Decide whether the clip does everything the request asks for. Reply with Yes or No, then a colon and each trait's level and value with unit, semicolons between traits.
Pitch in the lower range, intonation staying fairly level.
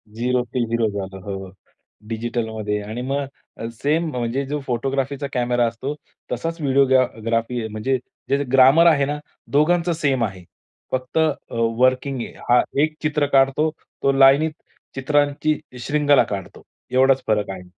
No: low, 130 Hz; average, 3.7 semitones